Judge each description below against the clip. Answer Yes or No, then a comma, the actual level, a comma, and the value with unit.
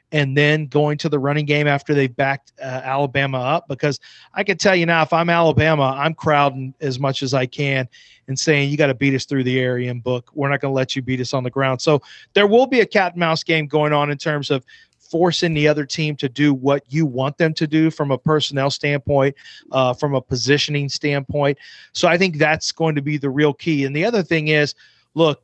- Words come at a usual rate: No, fast, 245 wpm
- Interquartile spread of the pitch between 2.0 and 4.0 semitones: Yes, narrow, 2.5 semitones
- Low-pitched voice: No, medium, 145 Hz